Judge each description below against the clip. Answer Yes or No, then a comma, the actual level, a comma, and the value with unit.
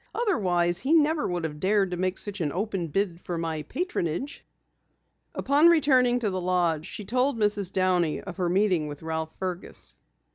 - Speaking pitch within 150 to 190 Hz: Yes, medium, 185 Hz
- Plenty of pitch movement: No, average, 4.8 semitones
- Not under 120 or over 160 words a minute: No, average, 175 wpm